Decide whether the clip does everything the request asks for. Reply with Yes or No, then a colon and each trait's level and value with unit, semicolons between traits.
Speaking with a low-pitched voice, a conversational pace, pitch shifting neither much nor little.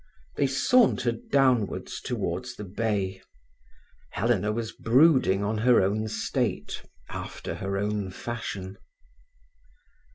No: low, 110 Hz; slow, 100 wpm; average, 3.4 semitones